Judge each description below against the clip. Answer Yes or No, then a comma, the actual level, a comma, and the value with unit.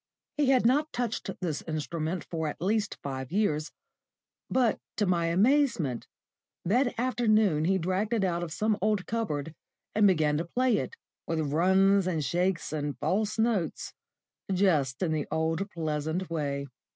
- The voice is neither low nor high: Yes, medium, 180 Hz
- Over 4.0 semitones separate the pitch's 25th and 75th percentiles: Yes, wide, 5.4 semitones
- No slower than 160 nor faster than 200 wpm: No, average, 150 wpm